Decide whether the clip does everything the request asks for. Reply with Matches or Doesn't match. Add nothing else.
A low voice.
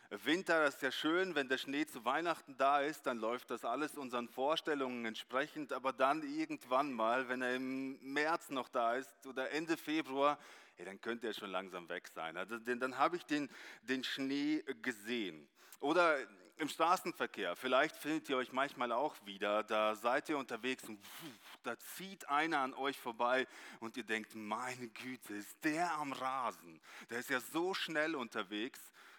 Matches